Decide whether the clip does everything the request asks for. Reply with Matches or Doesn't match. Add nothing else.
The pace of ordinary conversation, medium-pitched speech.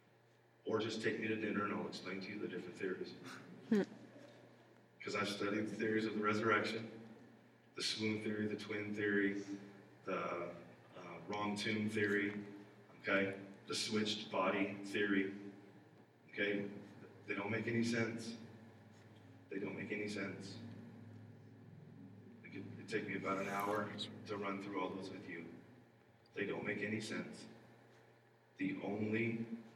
Doesn't match